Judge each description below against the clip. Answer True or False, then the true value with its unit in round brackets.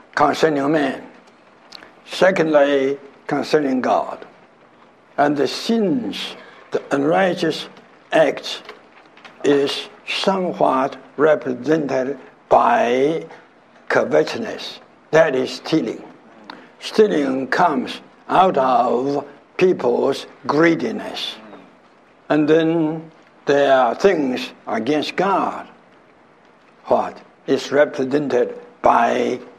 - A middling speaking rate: False (75 wpm)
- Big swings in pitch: False (2.8 semitones)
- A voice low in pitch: False (145 Hz)